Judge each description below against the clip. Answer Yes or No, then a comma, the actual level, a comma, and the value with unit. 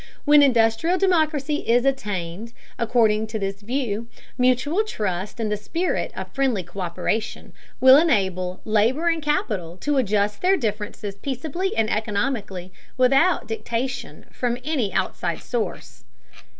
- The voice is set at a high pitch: Yes, high, 230 Hz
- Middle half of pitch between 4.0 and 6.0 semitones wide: Yes, average, 5.2 semitones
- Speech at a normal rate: No, slow, 125 wpm